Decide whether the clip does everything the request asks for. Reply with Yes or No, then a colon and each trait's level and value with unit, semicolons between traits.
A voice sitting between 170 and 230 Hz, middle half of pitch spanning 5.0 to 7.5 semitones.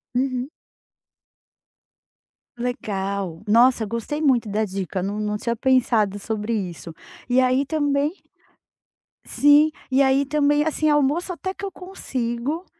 No: very high, 255 Hz; wide, 5.5 semitones